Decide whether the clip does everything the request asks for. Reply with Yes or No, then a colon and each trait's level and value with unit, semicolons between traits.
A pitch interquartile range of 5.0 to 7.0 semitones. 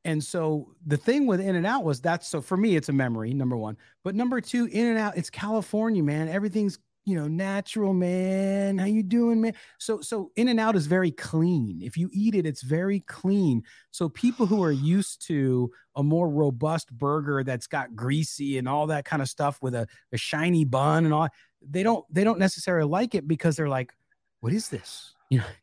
Yes: wide, 5.5 semitones